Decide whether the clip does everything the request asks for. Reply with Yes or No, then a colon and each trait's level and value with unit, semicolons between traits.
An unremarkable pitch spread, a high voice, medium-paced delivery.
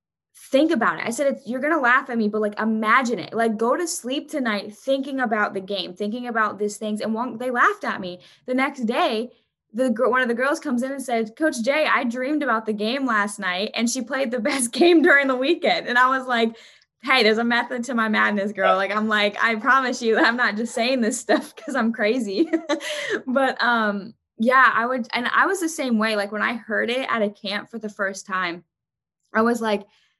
No: average, 3.6 semitones; high, 235 Hz; fast, 230 wpm